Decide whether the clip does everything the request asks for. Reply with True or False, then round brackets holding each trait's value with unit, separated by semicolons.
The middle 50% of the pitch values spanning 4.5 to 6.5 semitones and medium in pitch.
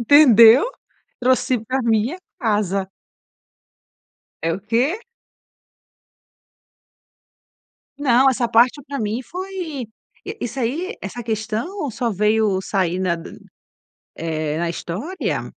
False (4.8 semitones; 230 Hz)